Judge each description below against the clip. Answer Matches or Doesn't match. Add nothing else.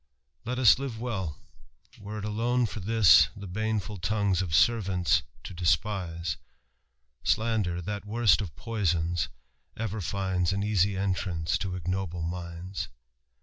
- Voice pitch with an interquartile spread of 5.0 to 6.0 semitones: Doesn't match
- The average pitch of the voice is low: Matches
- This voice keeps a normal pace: Doesn't match